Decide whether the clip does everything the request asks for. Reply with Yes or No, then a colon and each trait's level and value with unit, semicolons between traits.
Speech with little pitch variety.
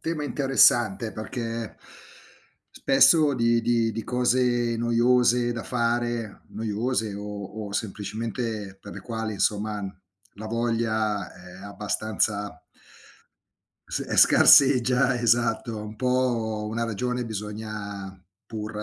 Yes: narrow, 2.3 semitones